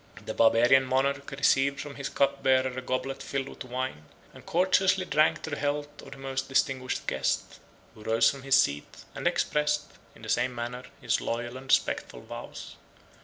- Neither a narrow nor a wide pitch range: No, narrow, 1.9 semitones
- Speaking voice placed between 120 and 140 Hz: Yes, low, 135 Hz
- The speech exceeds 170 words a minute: Yes, average, 180 wpm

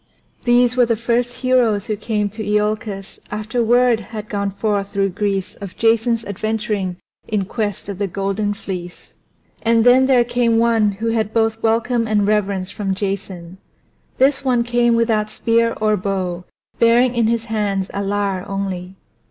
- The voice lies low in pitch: No, high, 215 Hz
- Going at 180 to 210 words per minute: No, average, 165 wpm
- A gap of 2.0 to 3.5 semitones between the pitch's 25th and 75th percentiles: Yes, average, 2.7 semitones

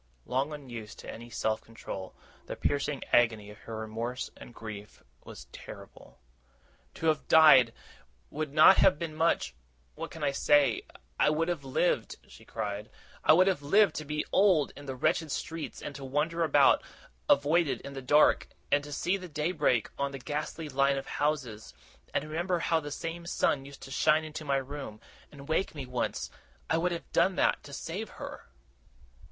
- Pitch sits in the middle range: Yes, medium, 145 Hz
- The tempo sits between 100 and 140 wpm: No, average, 185 wpm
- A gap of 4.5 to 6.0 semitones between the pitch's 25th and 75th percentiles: No, average, 3.6 semitones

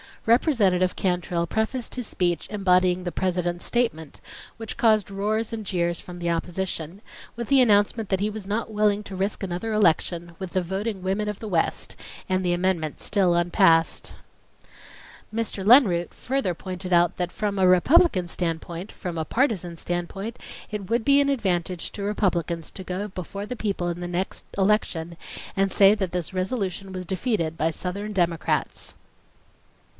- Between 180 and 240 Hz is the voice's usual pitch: Yes, high, 190 Hz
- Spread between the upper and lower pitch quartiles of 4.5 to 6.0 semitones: No, average, 3.3 semitones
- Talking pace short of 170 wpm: Yes, average, 160 wpm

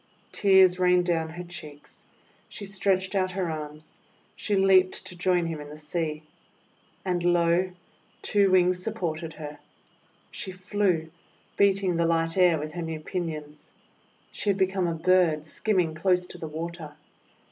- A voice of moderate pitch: Yes, medium, 175 Hz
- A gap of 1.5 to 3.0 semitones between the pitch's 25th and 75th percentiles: Yes, average, 2.7 semitones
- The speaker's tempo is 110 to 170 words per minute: Yes, average, 150 wpm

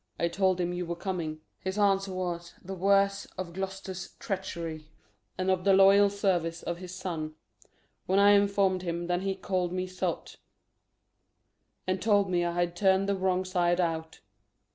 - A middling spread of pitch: No, narrow, 1.9 semitones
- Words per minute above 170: No, average, 165 wpm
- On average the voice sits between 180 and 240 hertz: Yes, medium, 185 Hz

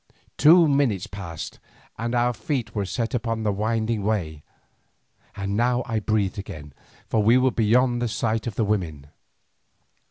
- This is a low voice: Yes, low, 110 Hz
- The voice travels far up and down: No, average, 3.3 semitones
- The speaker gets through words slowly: No, average, 155 wpm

